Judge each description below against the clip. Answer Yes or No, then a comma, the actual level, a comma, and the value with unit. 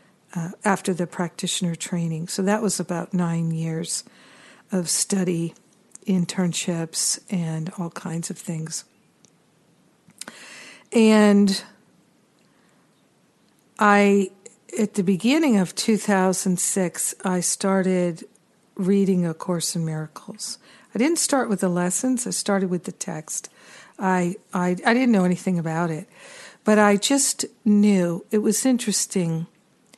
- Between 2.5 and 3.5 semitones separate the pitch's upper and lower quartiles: Yes, average, 3.1 semitones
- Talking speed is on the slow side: Yes, slow, 120 wpm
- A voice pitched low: No, high, 190 Hz